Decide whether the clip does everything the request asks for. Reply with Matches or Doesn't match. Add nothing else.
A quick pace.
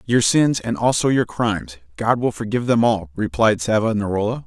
Doesn't match